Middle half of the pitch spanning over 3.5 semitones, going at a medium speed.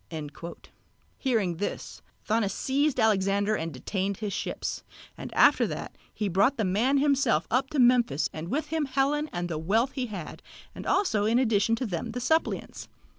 Yes: wide, 5.4 semitones; average, 170 wpm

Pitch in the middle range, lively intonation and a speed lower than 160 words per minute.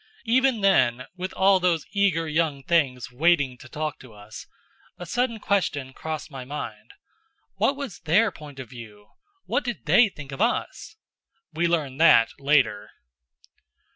Yes: medium, 160 Hz; wide, 6.7 semitones; average, 150 wpm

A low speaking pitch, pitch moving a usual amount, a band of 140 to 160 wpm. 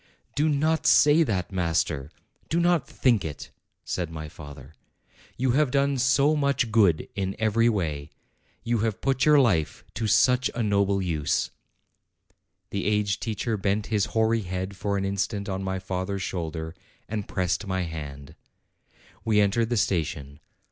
Yes: low, 100 Hz; average, 4.9 semitones; average, 155 wpm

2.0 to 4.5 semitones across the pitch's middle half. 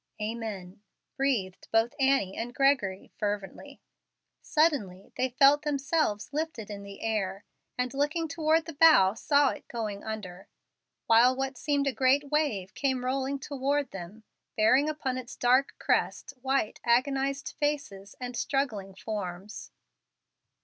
No: average, 5.2 semitones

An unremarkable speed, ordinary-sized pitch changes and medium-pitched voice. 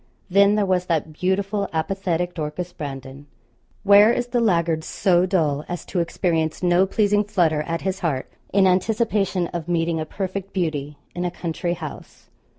Yes: average, 160 wpm; average, 3.5 semitones; medium, 180 Hz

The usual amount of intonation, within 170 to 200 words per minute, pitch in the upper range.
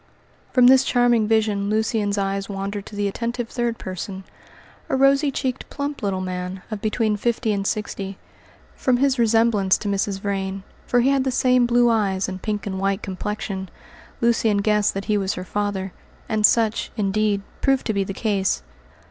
Yes: average, 3.2 semitones; average, 175 wpm; high, 210 Hz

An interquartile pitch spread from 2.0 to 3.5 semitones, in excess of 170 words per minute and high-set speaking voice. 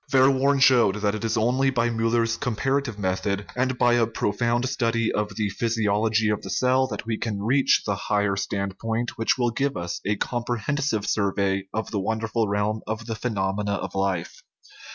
No: average, 2.8 semitones; average, 185 wpm; low, 110 Hz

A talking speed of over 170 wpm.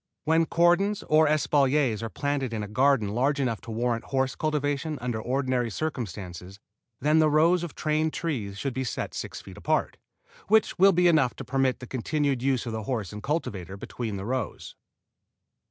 Yes: average, 180 wpm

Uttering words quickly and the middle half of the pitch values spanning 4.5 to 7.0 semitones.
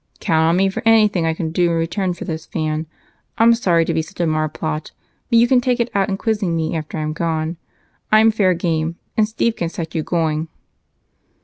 Yes: fast, 215 wpm; average, 4.8 semitones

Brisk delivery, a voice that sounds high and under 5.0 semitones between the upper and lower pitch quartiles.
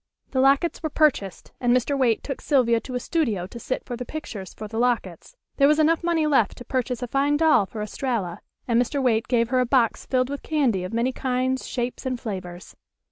Yes: fast, 220 wpm; very high, 250 Hz; average, 3.4 semitones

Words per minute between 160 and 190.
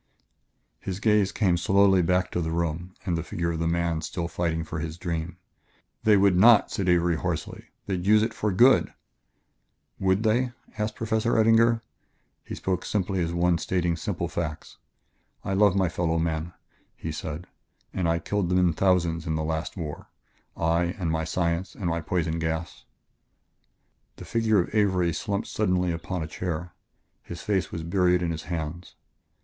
Yes: average, 170 wpm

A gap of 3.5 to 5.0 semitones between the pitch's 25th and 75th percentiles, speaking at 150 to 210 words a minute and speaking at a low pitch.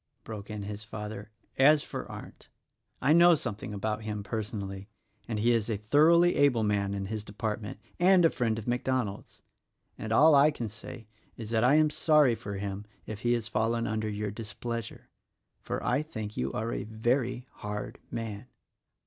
No: average, 3.1 semitones; average, 180 wpm; low, 110 Hz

